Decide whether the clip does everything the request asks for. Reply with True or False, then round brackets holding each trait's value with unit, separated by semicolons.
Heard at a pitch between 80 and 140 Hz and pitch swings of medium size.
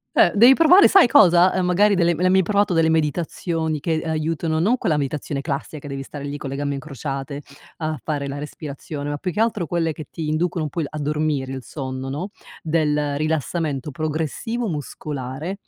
False (155 Hz; 3.3 semitones)